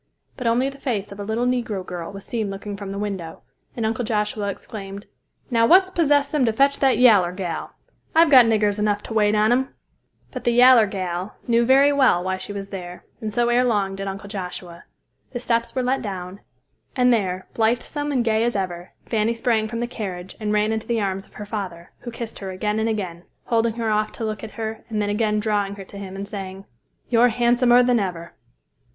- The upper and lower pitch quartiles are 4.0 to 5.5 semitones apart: No, average, 3.4 semitones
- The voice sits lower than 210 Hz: No, high, 215 Hz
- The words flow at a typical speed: No, fast, 220 wpm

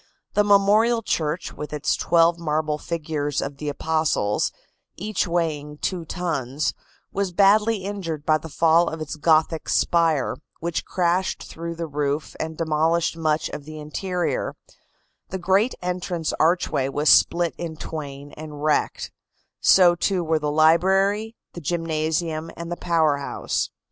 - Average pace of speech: Yes, average, 145 wpm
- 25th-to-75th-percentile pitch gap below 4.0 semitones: Yes, narrow, 2.6 semitones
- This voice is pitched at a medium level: Yes, medium, 165 Hz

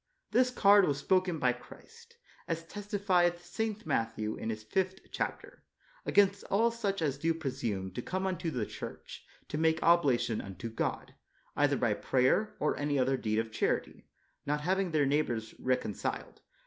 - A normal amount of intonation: No, wide, 7.5 semitones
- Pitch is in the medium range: Yes, medium, 160 Hz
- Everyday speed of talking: Yes, average, 160 wpm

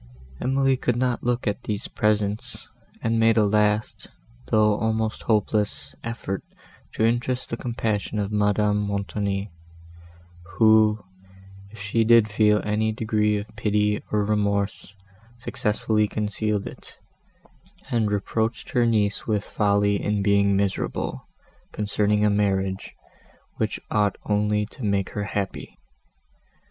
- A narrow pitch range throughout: Yes, narrow, 1.4 semitones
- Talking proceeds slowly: Yes, slow, 125 wpm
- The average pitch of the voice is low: Yes, low, 105 Hz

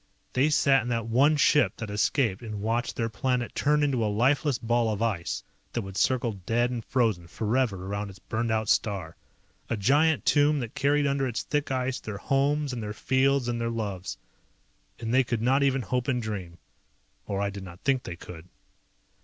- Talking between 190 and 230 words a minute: Yes, average, 195 wpm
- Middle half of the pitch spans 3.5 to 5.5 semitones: Yes, average, 4.3 semitones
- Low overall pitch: Yes, low, 120 Hz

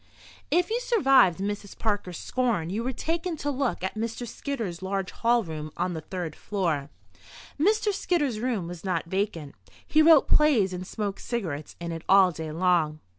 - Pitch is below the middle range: No, high, 200 Hz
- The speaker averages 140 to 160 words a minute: No, average, 175 wpm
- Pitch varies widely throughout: Yes, wide, 7.2 semitones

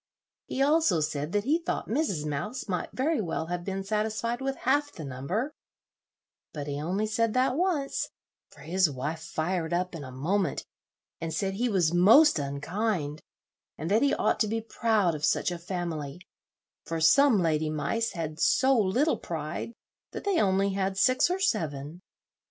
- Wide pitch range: Yes, wide, 6.5 semitones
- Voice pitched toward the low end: No, high, 190 Hz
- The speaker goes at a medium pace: Yes, average, 170 wpm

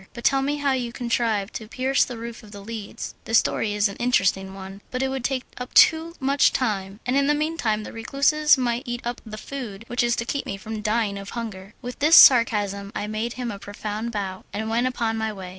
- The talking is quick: Yes, fast, 235 wpm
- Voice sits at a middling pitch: No, high, 230 Hz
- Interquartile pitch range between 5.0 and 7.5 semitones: No, average, 3.6 semitones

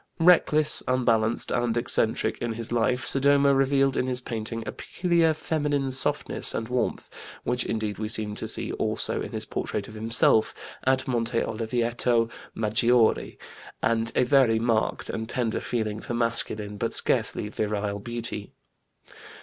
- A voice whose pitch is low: Yes, low, 115 Hz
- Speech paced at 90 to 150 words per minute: Yes, average, 145 wpm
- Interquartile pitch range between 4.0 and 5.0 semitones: No, narrow, 2.6 semitones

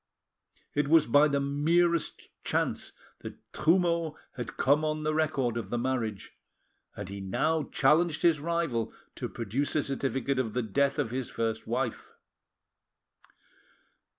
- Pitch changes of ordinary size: Yes, average, 4.6 semitones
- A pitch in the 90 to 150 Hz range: Yes, medium, 140 Hz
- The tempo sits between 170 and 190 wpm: No, average, 140 wpm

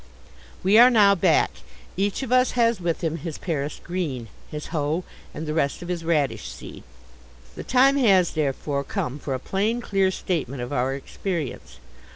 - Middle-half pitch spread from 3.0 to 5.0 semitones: No, wide, 5.5 semitones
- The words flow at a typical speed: Yes, average, 175 wpm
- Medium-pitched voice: Yes, medium, 170 Hz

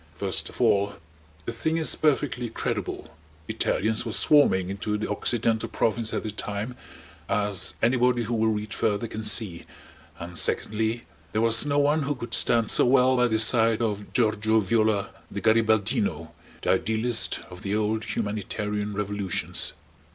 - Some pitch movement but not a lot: No, narrow, 2.1 semitones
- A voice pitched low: Yes, low, 110 Hz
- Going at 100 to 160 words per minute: Yes, average, 155 wpm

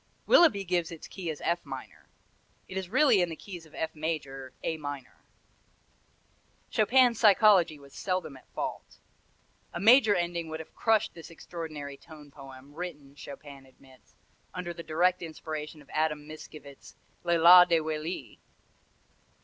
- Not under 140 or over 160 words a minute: Yes, average, 150 wpm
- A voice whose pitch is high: No, medium, 160 Hz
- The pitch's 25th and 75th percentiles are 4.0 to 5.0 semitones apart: No, average, 3.6 semitones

